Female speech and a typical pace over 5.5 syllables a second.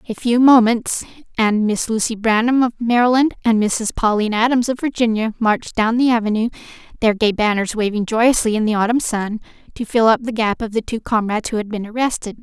Yes: female; 5.7 syllables/s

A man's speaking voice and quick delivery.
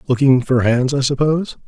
No: male; average, 180 wpm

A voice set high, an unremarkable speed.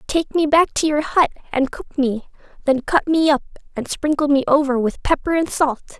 No: very high, 290 Hz; fast, 210 wpm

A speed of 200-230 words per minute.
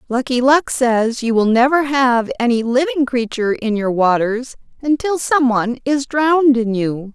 No: average, 160 wpm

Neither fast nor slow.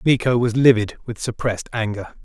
Yes: average, 160 wpm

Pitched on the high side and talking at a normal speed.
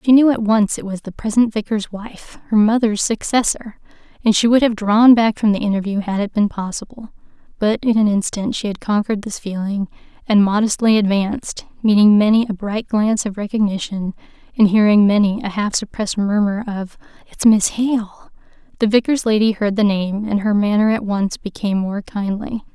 Yes: high, 210 Hz; average, 185 wpm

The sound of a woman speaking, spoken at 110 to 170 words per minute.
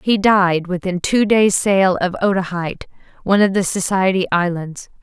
Yes: female; average, 155 wpm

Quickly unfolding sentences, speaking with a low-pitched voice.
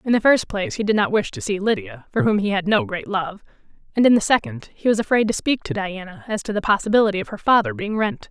No: fast, 275 wpm; high, 210 Hz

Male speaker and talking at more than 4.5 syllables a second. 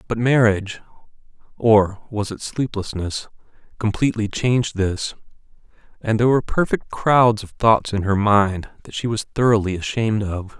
Yes: male; 5.0 syllables/s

